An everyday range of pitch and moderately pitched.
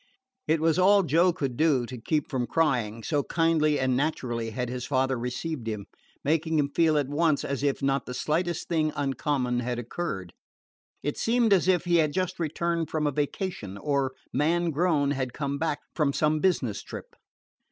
Yes: average, 4.1 semitones; medium, 145 Hz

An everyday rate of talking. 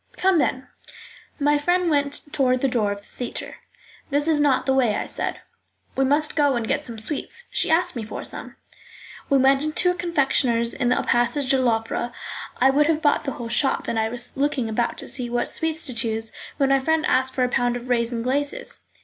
No: fast, 215 wpm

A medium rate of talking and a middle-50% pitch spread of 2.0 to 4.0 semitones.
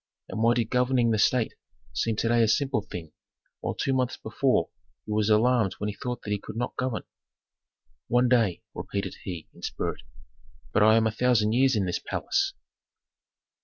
Yes: average, 185 wpm; average, 2.8 semitones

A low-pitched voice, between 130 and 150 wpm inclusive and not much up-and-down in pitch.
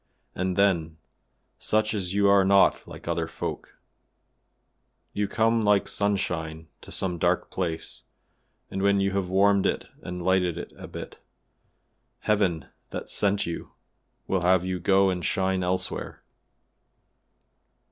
Yes: very low, 95 Hz; slow, 135 wpm; narrow, 2.0 semitones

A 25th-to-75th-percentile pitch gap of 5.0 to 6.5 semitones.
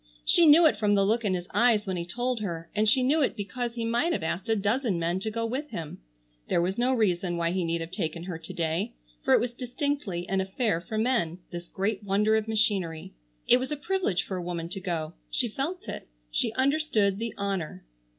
Yes: wide, 5.6 semitones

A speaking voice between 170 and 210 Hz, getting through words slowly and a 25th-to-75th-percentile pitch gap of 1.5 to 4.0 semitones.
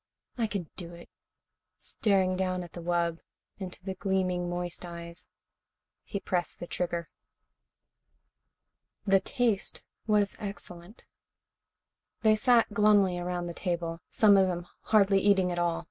Yes: medium, 185 Hz; slow, 130 wpm; narrow, 2.5 semitones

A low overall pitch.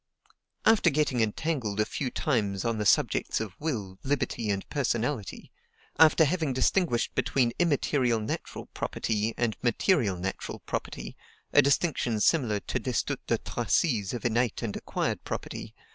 Yes: low, 120 Hz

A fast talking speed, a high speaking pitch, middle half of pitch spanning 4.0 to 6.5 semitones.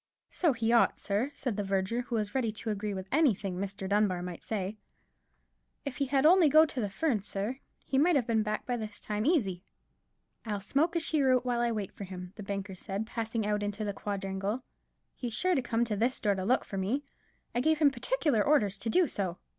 Yes: fast, 220 wpm; high, 220 Hz; average, 4.7 semitones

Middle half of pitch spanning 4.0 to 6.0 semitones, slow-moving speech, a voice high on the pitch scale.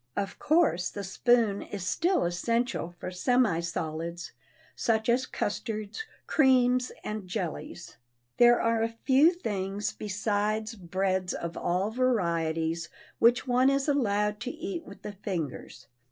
Yes: average, 5.2 semitones; slow, 130 wpm; high, 210 Hz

